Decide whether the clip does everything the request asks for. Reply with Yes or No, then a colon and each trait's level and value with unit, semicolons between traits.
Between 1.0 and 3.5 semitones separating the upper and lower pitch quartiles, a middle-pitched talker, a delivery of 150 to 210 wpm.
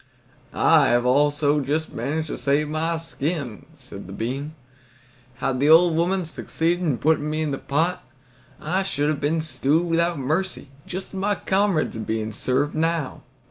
Yes: average, 3.2 semitones; medium, 155 Hz; average, 170 wpm